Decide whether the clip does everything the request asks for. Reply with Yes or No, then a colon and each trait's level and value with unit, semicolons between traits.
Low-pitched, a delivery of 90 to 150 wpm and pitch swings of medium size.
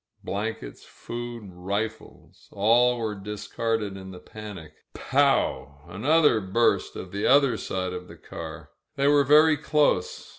Yes: low, 110 Hz; average, 140 wpm; average, 4.3 semitones